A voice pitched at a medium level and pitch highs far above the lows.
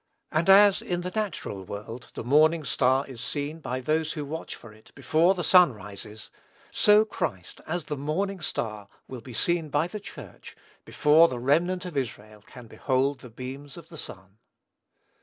Yes: medium, 145 Hz; wide, 5.9 semitones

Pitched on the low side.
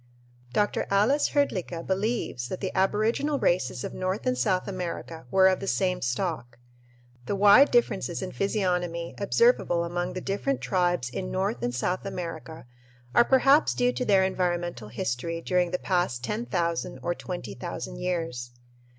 No: medium, 185 Hz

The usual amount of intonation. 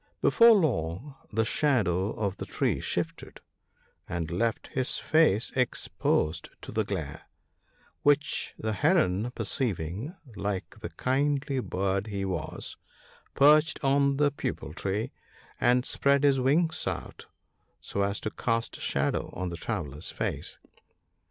No: wide, 6.7 semitones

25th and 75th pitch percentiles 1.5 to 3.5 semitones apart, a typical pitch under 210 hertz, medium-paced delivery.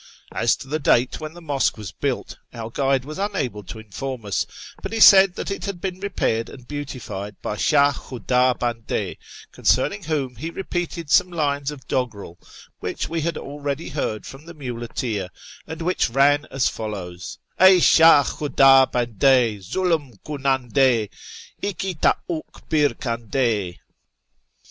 No: average, 5.3 semitones; low, 135 Hz; average, 155 wpm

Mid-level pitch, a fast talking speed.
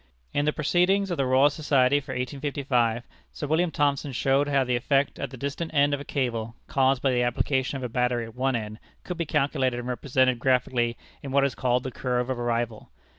No: low, 130 Hz; fast, 215 wpm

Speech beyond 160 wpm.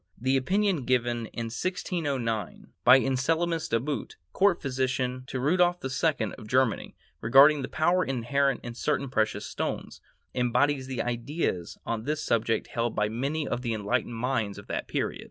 No: average, 155 wpm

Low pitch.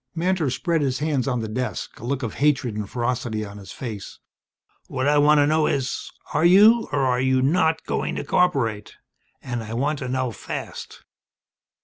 Yes: low, 130 Hz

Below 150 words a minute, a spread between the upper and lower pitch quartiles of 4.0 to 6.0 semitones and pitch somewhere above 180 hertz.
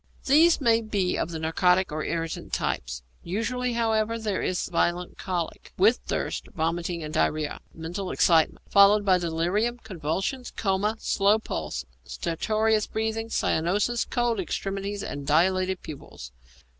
Yes: slow, 135 wpm; average, 4.9 semitones; high, 190 Hz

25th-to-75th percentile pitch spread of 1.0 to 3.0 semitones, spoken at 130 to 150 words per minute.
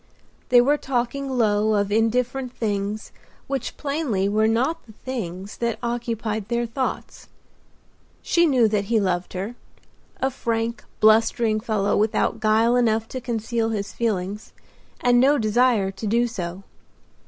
Yes: narrow, 2.6 semitones; slow, 135 wpm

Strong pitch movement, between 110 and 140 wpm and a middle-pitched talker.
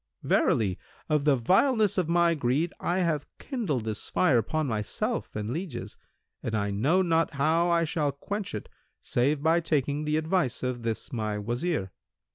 No: wide, 6.1 semitones; average, 165 wpm; medium, 150 Hz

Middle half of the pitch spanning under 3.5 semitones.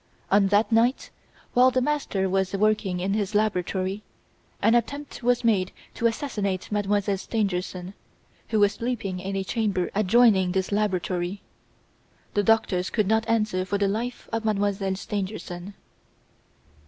Yes: average, 2.8 semitones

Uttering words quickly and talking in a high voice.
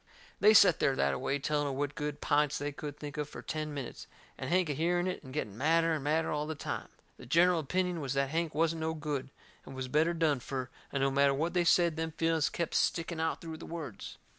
No: fast, 245 wpm; medium, 155 Hz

